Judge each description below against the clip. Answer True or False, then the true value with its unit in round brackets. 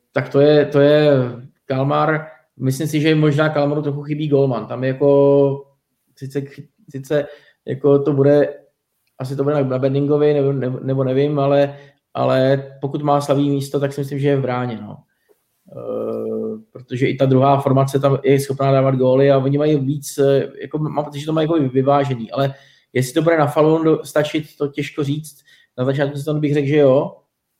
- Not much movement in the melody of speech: True (1.4 semitones)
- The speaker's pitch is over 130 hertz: True (140 Hz)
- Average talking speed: False (180 wpm)